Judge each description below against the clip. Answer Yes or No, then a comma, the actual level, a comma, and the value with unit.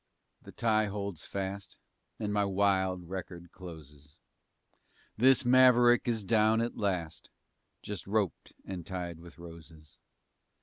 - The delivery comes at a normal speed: No, slow, 120 wpm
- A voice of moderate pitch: No, very low, 95 Hz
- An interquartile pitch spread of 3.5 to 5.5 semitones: Yes, average, 4.0 semitones